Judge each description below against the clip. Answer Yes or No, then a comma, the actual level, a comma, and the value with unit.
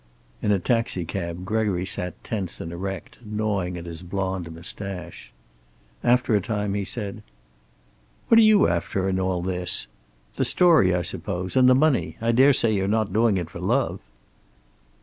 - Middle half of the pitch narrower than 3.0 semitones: No, average, 3.9 semitones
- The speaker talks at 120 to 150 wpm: No, average, 160 wpm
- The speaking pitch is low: Yes, low, 100 Hz